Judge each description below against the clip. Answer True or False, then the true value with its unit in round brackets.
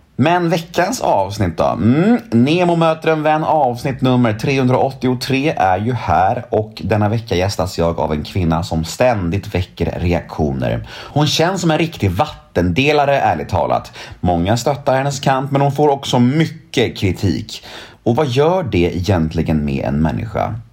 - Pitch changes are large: True (8.4 semitones)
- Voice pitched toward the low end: True (120 Hz)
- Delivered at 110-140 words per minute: False (155 wpm)